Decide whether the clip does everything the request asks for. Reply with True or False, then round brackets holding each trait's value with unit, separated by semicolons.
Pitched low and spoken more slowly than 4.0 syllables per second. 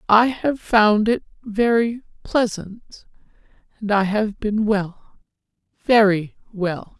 False (210 Hz; 3.2 syllables/s)